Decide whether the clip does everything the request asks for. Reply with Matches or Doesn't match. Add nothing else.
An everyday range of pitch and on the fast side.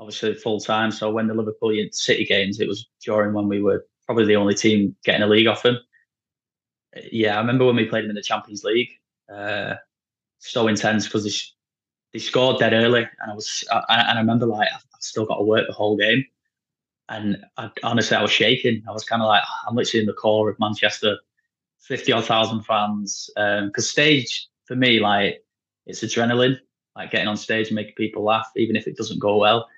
Doesn't match